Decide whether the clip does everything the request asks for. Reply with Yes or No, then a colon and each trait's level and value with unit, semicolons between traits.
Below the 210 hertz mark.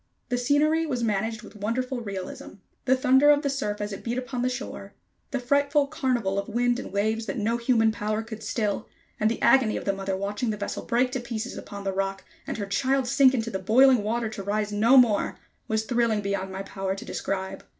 No: high, 225 Hz